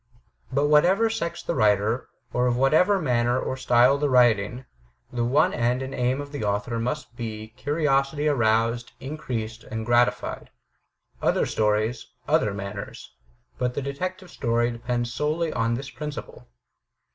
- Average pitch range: Yes, average, 3.7 semitones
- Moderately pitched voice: No, low, 125 Hz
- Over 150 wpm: No, average, 145 wpm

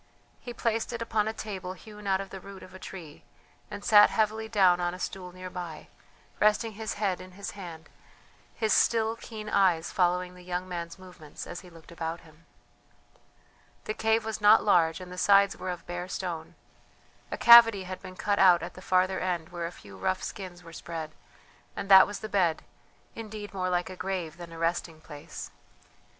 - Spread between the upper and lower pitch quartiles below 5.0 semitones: Yes, average, 2.9 semitones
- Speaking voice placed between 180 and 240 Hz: Yes, medium, 185 Hz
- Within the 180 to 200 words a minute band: Yes, average, 195 wpm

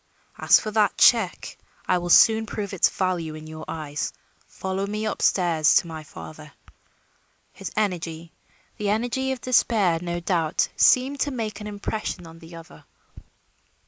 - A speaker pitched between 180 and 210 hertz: Yes, medium, 185 Hz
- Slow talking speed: No, average, 155 wpm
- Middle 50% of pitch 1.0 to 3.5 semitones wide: No, average, 4.7 semitones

